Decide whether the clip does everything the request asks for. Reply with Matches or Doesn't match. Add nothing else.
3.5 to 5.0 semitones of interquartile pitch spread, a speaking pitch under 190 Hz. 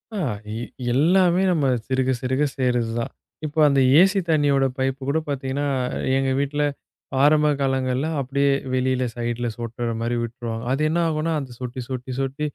Doesn't match